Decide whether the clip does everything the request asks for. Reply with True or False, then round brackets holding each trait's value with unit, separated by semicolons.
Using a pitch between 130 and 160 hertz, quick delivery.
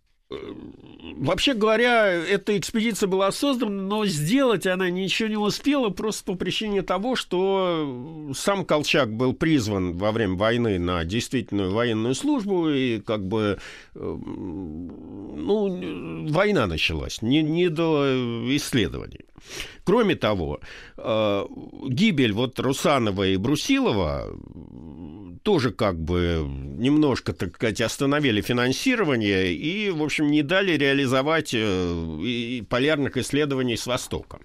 False (140 Hz; 110 wpm)